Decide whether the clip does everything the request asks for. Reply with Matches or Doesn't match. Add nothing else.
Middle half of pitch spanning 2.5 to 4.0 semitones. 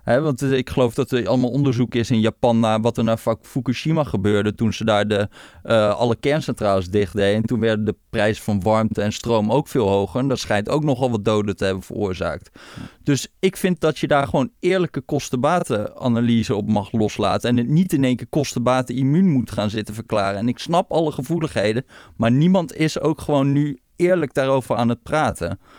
Doesn't match